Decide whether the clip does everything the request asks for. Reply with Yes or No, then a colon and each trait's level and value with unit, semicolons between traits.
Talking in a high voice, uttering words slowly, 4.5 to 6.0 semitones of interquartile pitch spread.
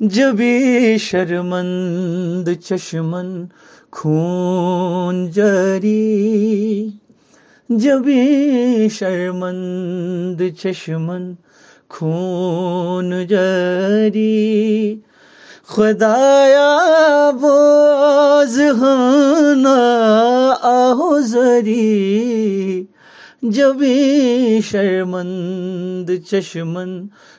Yes: high, 210 Hz; slow, 35 wpm; wide, 5.6 semitones